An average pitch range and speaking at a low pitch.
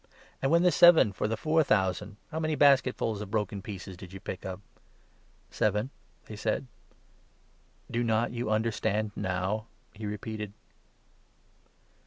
Yes: average, 3.2 semitones; low, 110 Hz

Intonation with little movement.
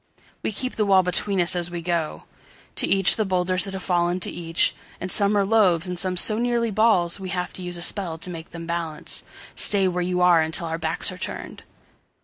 Yes: narrow, 2.2 semitones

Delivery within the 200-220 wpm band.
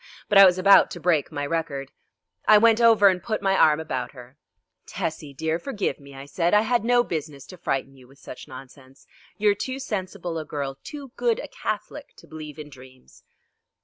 Yes: fast, 205 wpm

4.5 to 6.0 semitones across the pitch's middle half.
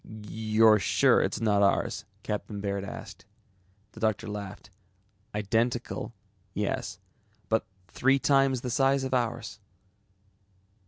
No: average, 3.1 semitones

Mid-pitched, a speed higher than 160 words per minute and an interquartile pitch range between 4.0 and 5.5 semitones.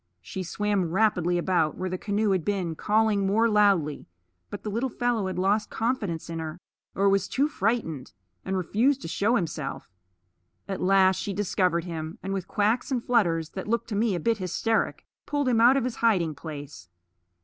No: high, 195 Hz; average, 185 wpm; average, 4.5 semitones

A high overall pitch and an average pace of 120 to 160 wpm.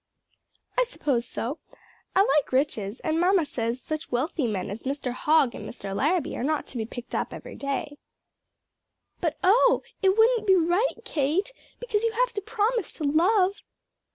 No: very high, 315 Hz; average, 170 wpm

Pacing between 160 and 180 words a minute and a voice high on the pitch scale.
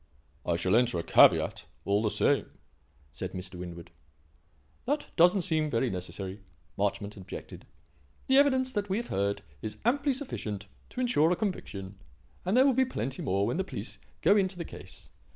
No: average, 170 wpm; medium, 145 Hz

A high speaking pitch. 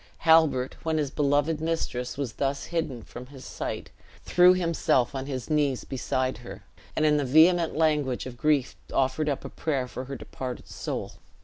No: medium, 140 Hz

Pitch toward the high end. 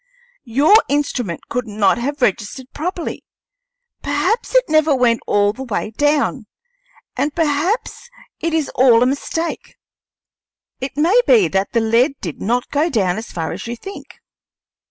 Yes: very high, 265 Hz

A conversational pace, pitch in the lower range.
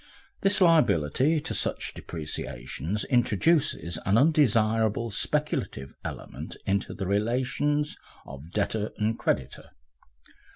No: slow, 95 wpm; low, 110 Hz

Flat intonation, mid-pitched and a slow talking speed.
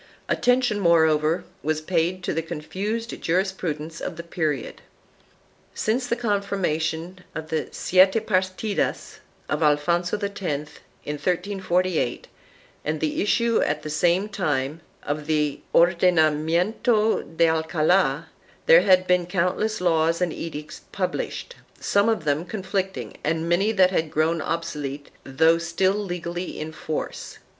No: average, 3.5 semitones; medium, 170 Hz; slow, 130 wpm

